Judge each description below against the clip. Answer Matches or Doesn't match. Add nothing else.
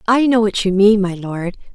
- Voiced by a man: Doesn't match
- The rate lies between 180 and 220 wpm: Doesn't match